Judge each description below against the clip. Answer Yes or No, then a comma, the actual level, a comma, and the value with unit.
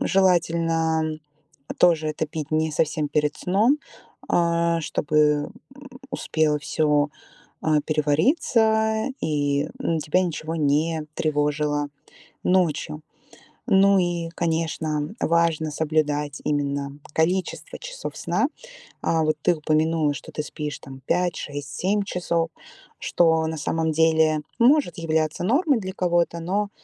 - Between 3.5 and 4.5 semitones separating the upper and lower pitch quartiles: No, average, 2.7 semitones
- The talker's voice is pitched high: No, medium, 160 Hz